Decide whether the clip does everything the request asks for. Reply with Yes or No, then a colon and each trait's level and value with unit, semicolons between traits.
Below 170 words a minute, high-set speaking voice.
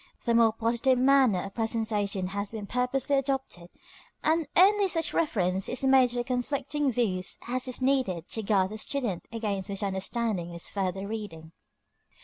Yes: average, 155 wpm; high, 230 Hz